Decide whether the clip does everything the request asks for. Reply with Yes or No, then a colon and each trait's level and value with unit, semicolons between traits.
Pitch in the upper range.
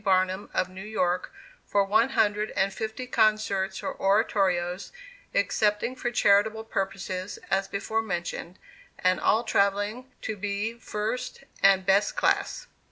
Yes: high, 200 Hz